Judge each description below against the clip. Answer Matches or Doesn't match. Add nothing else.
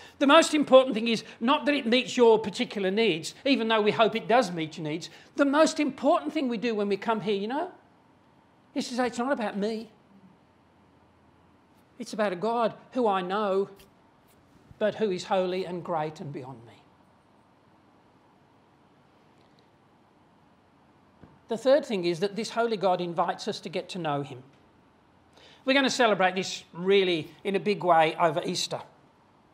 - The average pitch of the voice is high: Matches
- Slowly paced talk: Doesn't match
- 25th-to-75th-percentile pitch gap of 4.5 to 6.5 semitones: Matches